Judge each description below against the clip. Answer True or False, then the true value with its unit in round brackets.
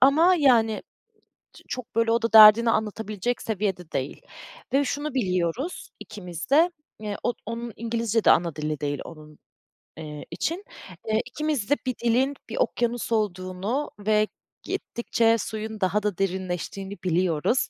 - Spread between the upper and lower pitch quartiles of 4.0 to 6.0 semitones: True (4.7 semitones)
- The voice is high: True (220 Hz)